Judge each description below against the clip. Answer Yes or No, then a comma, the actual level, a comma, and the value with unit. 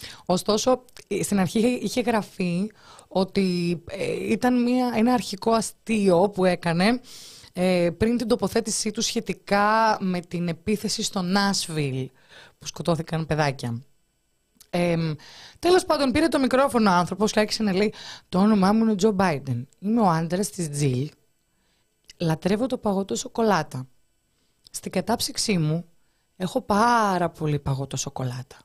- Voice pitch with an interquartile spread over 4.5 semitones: Yes, average, 5.1 semitones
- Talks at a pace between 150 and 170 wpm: No, average, 130 wpm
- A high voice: Yes, high, 195 Hz